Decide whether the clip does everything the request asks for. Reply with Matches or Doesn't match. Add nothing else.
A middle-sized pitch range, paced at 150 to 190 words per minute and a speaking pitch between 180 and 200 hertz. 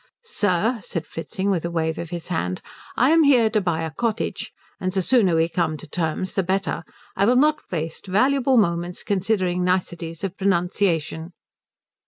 Matches